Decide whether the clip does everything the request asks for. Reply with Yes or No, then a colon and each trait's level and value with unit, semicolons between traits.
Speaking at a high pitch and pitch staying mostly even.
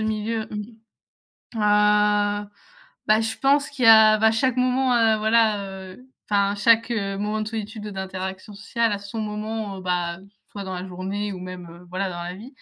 Yes: high, 210 Hz; narrow, 2.3 semitones